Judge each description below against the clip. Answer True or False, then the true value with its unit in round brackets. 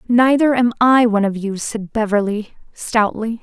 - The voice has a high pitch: True (225 Hz)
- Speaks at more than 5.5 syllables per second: False (4.6 syllables/s)